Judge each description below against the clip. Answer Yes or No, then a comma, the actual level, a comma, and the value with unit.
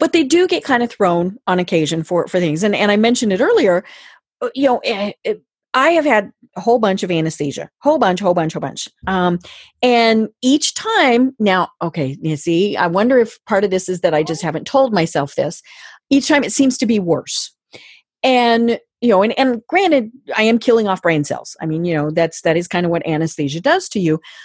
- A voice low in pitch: No, high, 205 Hz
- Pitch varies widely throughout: Yes, wide, 7.0 semitones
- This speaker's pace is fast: Yes, fast, 220 wpm